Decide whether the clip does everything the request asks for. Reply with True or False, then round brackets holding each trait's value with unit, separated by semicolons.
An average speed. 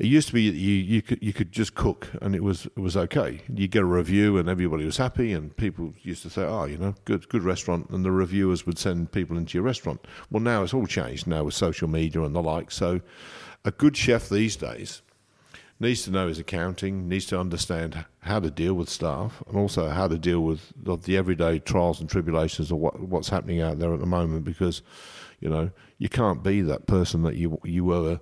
False (240 wpm)